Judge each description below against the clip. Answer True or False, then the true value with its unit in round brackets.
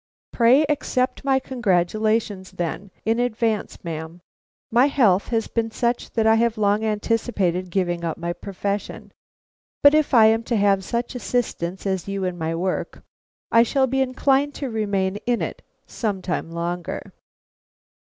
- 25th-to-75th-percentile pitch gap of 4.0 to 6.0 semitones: True (4.5 semitones)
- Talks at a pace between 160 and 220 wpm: False (150 wpm)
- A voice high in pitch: True (215 Hz)